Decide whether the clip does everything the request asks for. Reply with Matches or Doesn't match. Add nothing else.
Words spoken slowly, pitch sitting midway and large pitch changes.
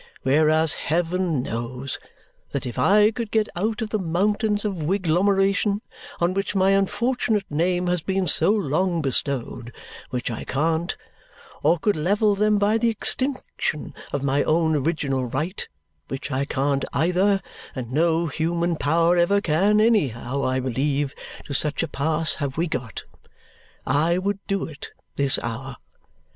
Doesn't match